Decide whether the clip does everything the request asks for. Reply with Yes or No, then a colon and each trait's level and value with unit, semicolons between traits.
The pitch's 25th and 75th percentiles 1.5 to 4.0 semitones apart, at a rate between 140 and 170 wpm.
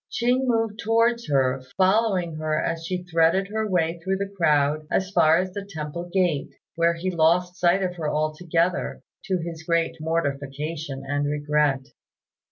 Yes: average, 3.5 semitones; average, 160 wpm